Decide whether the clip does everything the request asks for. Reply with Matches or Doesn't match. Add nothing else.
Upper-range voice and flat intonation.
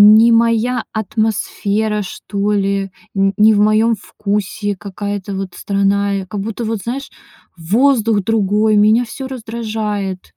Matches